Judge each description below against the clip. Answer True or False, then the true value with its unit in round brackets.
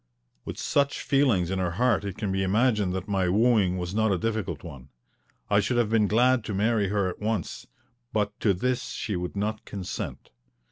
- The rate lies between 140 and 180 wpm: False (195 wpm)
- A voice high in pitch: False (105 Hz)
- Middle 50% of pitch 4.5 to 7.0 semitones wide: False (3.3 semitones)